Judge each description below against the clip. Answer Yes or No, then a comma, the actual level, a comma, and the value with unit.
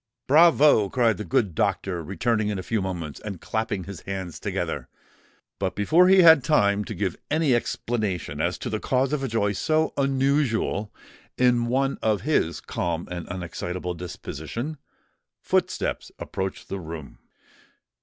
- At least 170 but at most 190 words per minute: No, average, 150 wpm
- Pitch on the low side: Yes, low, 105 Hz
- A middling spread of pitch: No, wide, 6.4 semitones